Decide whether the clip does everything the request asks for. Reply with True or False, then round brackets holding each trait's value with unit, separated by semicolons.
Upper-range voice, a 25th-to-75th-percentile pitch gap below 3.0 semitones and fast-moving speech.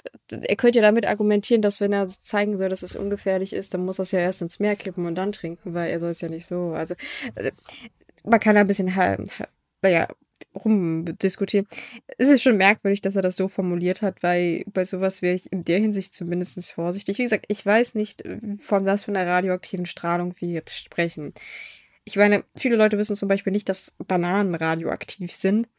True (195 Hz; 2.6 semitones; 205 wpm)